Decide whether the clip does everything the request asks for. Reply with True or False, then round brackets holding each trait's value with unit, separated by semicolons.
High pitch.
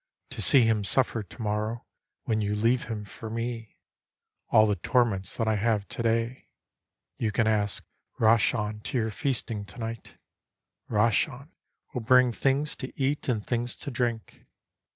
False (115 Hz)